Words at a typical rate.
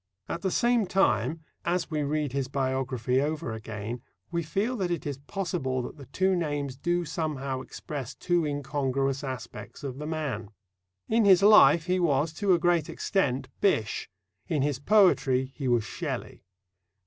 Yes: average, 160 wpm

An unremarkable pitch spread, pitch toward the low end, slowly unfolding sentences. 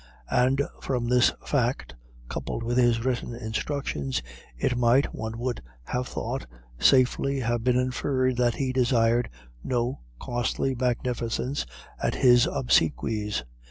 No: narrow, 1.6 semitones; low, 125 Hz; slow, 125 wpm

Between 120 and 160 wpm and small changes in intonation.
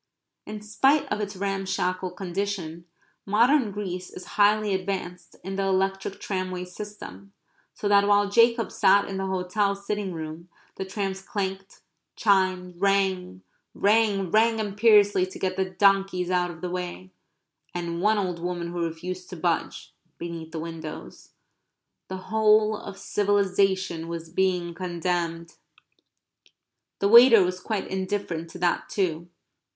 Yes: slow, 135 wpm; narrow, 2.2 semitones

